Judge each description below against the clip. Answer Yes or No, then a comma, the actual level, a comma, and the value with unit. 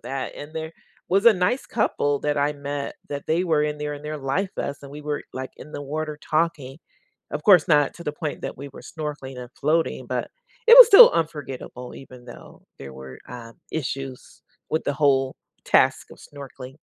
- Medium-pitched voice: Yes, medium, 145 Hz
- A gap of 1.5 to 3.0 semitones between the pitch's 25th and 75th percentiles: Yes, average, 2.7 semitones